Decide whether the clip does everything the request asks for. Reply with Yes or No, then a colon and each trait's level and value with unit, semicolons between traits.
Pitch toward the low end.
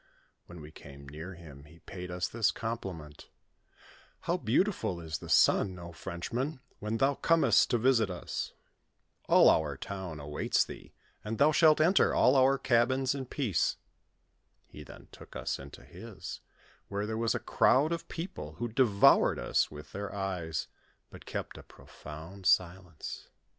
Yes: low, 100 Hz